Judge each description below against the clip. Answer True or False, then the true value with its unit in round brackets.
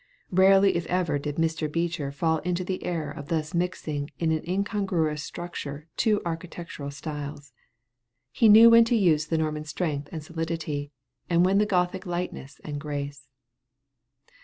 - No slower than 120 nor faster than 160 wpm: True (155 wpm)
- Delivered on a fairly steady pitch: False (3.3 semitones)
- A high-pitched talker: False (165 Hz)